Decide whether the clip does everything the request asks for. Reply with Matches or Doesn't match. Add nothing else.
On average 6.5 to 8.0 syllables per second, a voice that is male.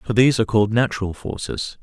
Matches